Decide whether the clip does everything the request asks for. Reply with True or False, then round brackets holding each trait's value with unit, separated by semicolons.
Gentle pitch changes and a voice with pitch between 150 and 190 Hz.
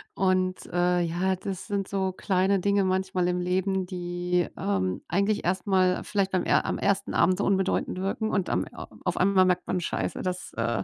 True (1.4 semitones; 185 Hz)